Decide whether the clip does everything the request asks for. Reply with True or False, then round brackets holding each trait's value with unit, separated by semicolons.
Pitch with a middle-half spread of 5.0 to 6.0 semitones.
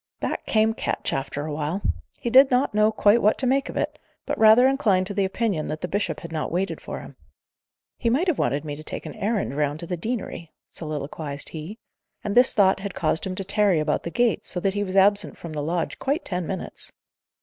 True (5.6 semitones)